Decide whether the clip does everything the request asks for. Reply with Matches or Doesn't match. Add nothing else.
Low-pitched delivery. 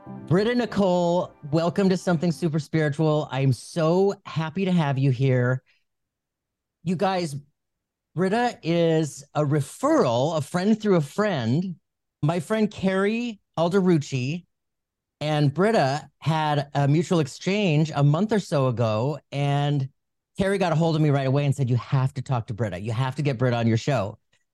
Doesn't match